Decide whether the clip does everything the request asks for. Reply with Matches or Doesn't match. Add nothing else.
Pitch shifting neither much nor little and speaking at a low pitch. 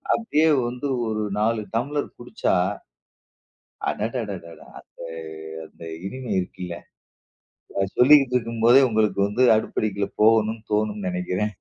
Matches